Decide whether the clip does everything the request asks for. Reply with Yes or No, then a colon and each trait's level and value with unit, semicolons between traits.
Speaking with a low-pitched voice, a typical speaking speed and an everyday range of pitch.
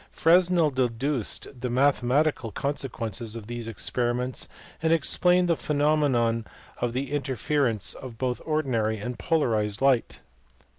No: low, 130 Hz; slow, 115 wpm; average, 4.3 semitones